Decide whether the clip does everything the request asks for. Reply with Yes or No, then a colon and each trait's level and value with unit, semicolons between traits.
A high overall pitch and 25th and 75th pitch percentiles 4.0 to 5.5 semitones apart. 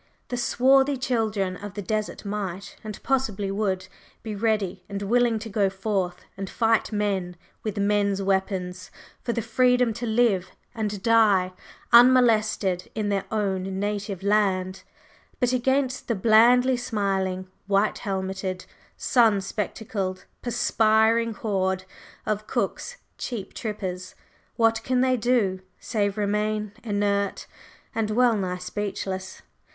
No: high, 210 Hz; average, 3.0 semitones